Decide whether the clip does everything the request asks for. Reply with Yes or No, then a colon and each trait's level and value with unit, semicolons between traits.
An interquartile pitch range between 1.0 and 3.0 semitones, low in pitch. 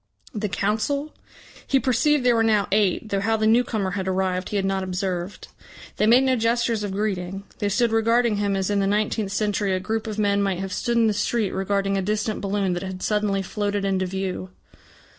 No: narrow, 2.5 semitones; high, 205 Hz